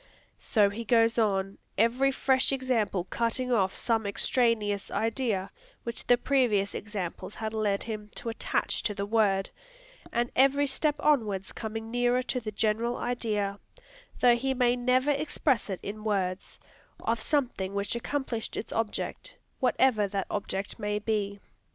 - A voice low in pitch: No, high, 225 Hz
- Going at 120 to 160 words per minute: Yes, average, 145 wpm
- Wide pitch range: No, average, 3.4 semitones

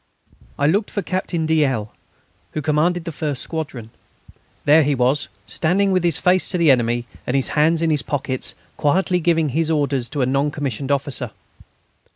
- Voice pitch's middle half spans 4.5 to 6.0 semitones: No, average, 3.5 semitones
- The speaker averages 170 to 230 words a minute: Yes, average, 180 wpm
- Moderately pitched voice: Yes, medium, 150 Hz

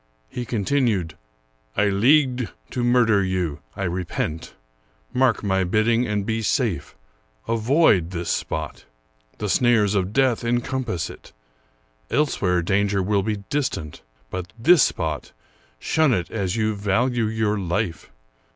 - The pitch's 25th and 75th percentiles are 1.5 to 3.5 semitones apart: No, average, 4.8 semitones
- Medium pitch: No, low, 105 Hz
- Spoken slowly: Yes, slow, 130 wpm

